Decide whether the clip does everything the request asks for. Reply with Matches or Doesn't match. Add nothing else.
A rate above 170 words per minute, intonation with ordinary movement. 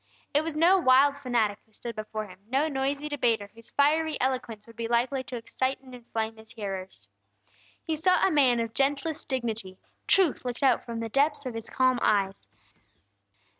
Matches